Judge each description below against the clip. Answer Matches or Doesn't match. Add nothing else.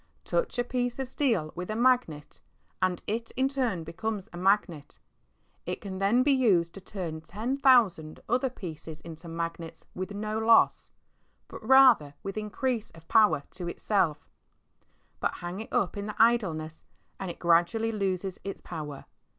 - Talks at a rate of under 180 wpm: Matches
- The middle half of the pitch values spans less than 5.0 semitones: Doesn't match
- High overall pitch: Matches